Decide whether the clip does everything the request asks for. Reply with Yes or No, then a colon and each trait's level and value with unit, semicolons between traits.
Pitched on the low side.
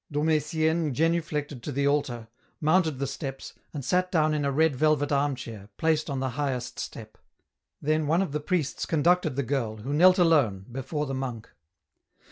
No: medium, 145 Hz